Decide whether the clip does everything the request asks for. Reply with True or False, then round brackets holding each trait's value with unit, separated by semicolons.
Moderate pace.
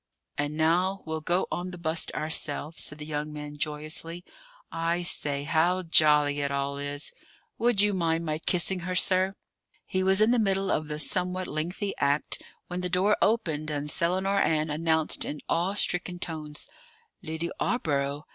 True (165 wpm)